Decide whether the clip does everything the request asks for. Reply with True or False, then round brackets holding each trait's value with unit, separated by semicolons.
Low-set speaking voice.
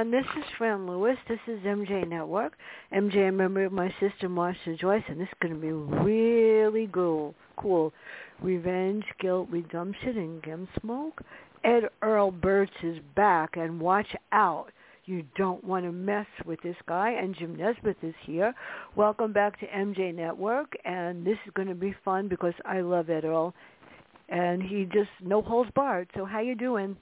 False (195 Hz)